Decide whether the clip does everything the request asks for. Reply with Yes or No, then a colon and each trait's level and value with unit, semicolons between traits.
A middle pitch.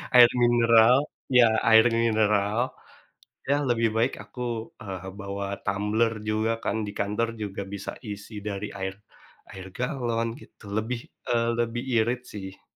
No: low, 110 Hz